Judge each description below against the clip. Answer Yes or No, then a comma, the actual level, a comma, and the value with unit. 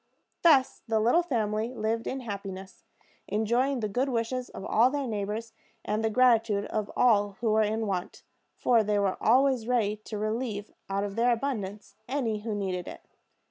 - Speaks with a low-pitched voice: No, high, 220 Hz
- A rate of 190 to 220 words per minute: No, average, 175 wpm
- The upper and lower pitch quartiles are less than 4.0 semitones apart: Yes, average, 3.0 semitones